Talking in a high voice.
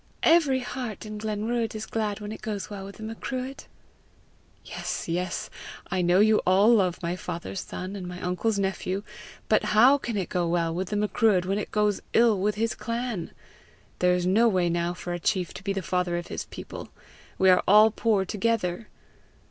Yes: high, 200 Hz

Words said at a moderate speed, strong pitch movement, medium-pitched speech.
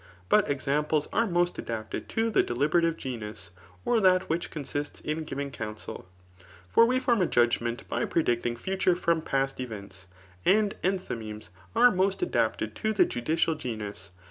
Yes: average, 160 wpm; wide, 7.7 semitones; medium, 150 Hz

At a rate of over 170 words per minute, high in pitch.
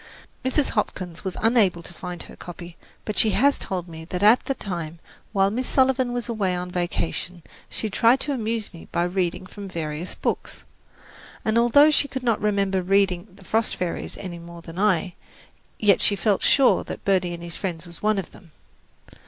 Yes: average, 195 wpm; high, 195 Hz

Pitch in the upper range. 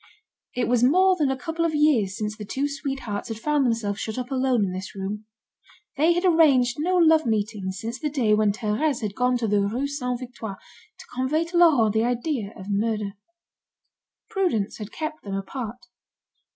Yes: high, 245 Hz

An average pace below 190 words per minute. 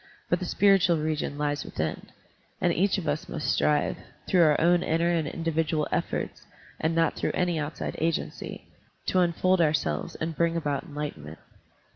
Yes: average, 160 wpm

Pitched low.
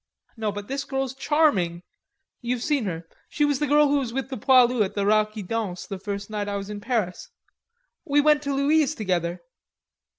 No: high, 230 Hz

